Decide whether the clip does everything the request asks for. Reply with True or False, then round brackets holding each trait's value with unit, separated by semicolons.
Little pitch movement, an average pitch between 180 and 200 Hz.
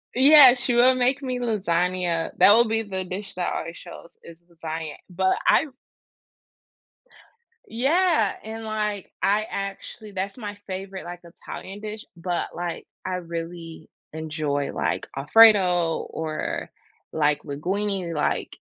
False (4.6 semitones; 190 Hz)